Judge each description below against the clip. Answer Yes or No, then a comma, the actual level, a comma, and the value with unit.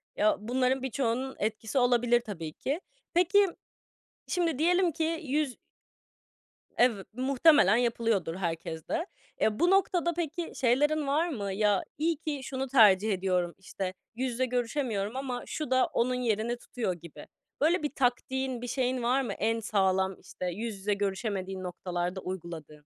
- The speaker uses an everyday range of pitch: No, wide, 5.8 semitones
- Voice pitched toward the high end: Yes, high, 240 Hz